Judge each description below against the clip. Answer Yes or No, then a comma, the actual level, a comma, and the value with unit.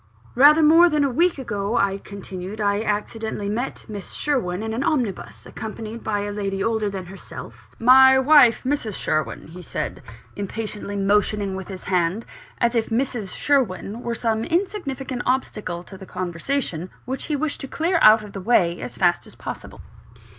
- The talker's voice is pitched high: Yes, high, 220 Hz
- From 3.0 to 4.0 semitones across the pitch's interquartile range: No, average, 5.1 semitones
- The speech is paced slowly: No, average, 175 wpm